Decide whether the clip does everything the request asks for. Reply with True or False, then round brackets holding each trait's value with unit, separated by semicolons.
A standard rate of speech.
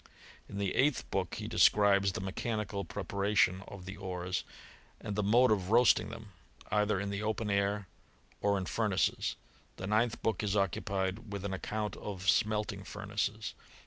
True (165 wpm)